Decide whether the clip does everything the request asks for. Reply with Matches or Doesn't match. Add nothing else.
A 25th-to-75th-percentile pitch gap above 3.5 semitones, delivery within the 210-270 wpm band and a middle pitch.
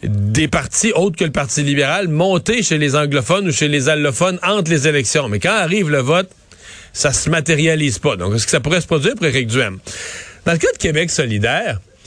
Matches